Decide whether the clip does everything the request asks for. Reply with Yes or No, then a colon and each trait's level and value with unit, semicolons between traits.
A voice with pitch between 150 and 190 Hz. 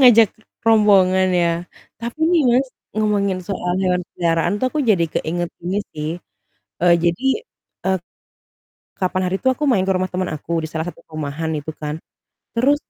Yes: medium, 185 Hz